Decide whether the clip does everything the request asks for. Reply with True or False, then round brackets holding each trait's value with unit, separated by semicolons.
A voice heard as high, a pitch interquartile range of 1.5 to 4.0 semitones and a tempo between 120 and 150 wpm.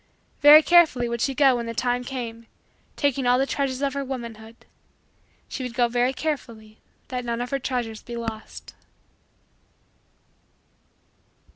True (245 Hz; 2.6 semitones; 145 wpm)